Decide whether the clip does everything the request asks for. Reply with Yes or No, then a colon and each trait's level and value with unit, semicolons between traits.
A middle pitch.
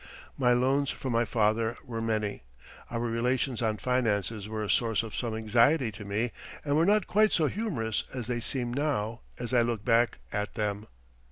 No: low, 115 Hz